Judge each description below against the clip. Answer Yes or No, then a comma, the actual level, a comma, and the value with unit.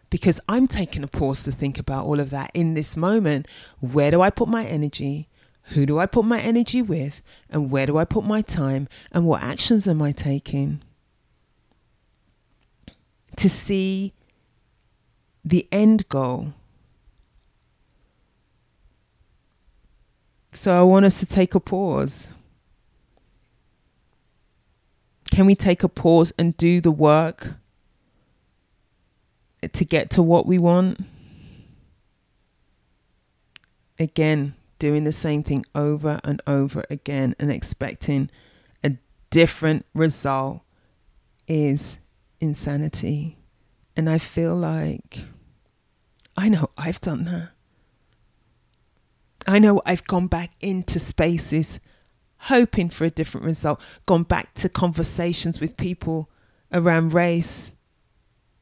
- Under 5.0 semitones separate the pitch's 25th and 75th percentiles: Yes, average, 4.3 semitones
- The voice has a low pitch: No, medium, 155 Hz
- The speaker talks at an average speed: No, slow, 115 wpm